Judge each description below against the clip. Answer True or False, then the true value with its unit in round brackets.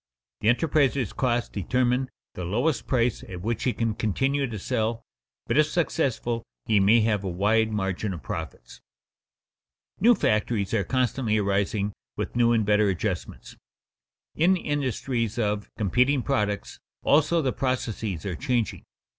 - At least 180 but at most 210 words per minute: False (140 wpm)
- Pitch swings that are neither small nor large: True (4.0 semitones)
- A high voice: False (115 Hz)